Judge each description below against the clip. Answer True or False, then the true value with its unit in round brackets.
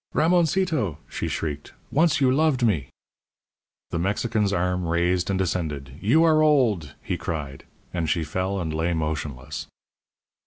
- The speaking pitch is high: False (90 Hz)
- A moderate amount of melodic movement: False (8.4 semitones)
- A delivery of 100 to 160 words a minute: True (140 wpm)